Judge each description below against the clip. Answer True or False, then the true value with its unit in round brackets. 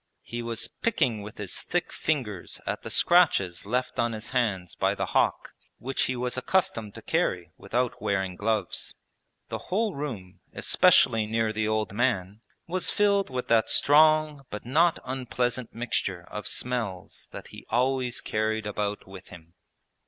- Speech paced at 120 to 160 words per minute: True (155 wpm)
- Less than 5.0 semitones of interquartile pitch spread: True (4.0 semitones)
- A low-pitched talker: True (115 Hz)